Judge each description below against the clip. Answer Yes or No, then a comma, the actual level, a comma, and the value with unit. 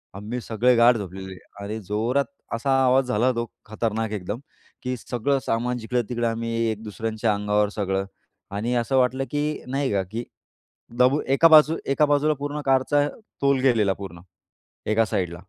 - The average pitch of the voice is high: No, low, 115 Hz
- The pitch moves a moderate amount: Yes, average, 4.0 semitones